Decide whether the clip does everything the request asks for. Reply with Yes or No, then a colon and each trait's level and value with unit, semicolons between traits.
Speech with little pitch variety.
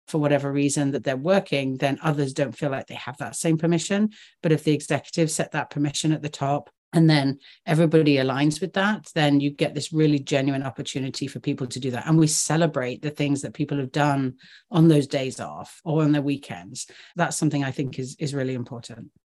Yes: narrow, 2.2 semitones